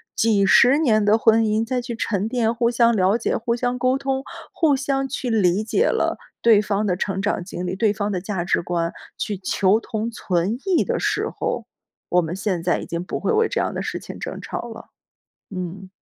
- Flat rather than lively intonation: No, average, 4.1 semitones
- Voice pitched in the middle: No, high, 215 Hz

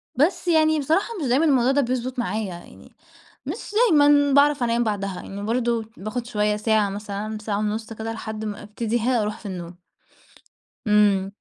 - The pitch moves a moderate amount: Yes, average, 3.7 semitones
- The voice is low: No, high, 225 Hz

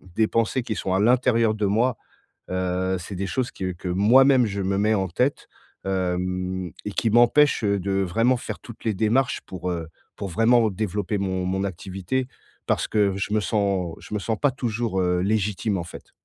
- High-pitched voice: No, low, 100 Hz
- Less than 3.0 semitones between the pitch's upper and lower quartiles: No, average, 3.6 semitones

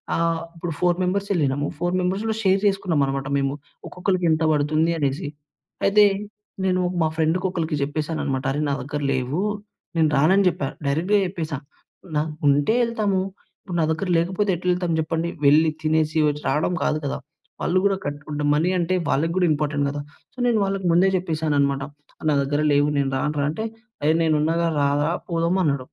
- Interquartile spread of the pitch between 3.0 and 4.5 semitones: Yes, average, 3.6 semitones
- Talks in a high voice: No, medium, 160 Hz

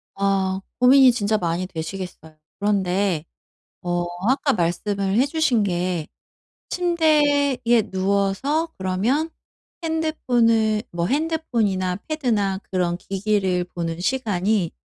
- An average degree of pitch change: No, wide, 6.3 semitones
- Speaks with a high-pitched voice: Yes, high, 200 Hz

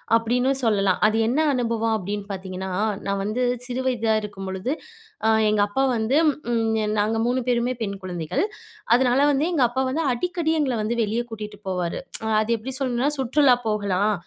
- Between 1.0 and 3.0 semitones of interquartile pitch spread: No, average, 3.8 semitones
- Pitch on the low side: No, high, 225 Hz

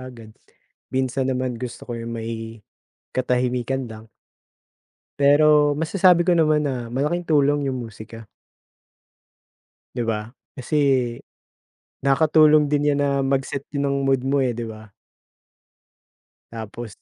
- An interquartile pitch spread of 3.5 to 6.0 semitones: Yes, average, 3.8 semitones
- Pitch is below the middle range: Yes, low, 130 Hz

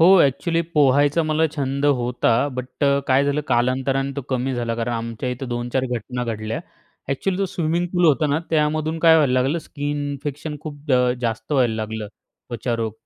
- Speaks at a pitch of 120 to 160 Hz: Yes, low, 135 Hz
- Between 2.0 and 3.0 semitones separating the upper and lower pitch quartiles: No, average, 3.6 semitones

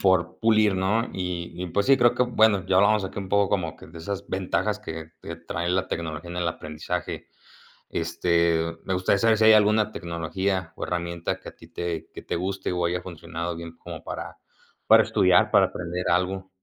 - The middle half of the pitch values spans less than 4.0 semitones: Yes, average, 2.9 semitones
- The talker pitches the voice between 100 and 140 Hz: No, very low, 90 Hz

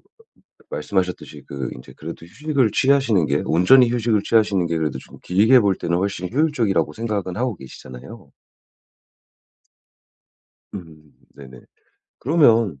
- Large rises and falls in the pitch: Yes, wide, 6.6 semitones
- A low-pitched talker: Yes, low, 100 Hz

